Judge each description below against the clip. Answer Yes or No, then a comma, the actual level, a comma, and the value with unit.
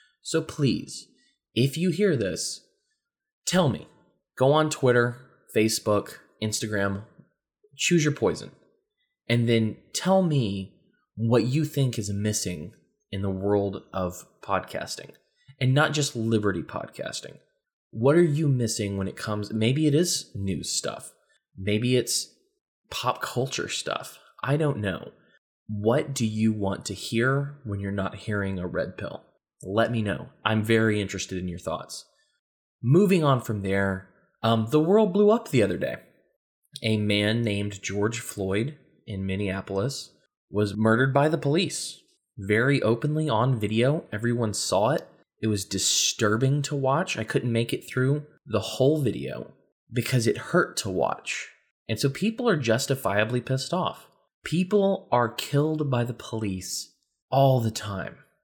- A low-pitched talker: Yes, low, 120 Hz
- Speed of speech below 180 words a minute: Yes, average, 145 wpm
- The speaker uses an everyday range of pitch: No, wide, 6.0 semitones